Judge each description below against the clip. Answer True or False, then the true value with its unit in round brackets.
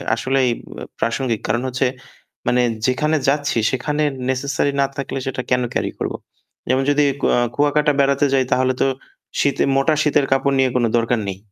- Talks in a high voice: False (135 Hz)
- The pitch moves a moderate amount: False (2.0 semitones)